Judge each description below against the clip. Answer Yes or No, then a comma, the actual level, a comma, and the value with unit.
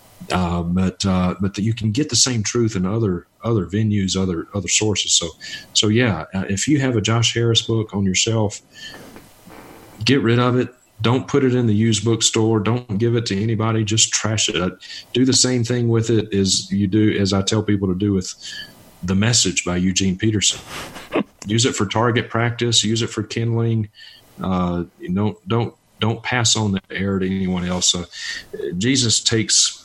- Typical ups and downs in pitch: Yes, average, 3.0 semitones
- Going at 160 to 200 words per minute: Yes, average, 195 wpm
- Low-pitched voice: Yes, low, 110 Hz